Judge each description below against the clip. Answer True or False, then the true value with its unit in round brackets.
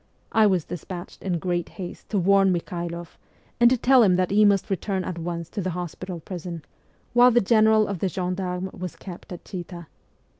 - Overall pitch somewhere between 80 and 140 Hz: False (185 Hz)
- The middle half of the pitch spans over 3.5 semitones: False (2.4 semitones)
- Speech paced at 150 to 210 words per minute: True (190 wpm)